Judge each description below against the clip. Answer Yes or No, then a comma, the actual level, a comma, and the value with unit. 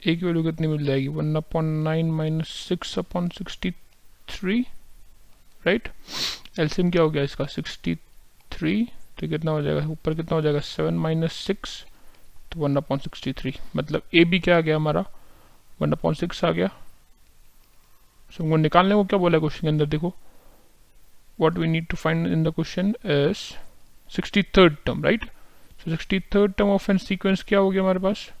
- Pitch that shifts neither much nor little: Yes, average, 3.4 semitones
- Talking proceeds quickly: No, average, 125 wpm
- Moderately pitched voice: Yes, medium, 165 Hz